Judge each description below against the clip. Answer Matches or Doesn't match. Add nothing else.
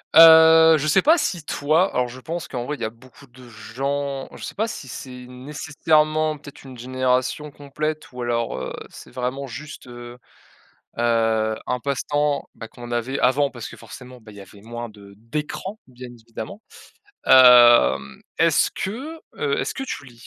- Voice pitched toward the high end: Doesn't match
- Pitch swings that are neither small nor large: Matches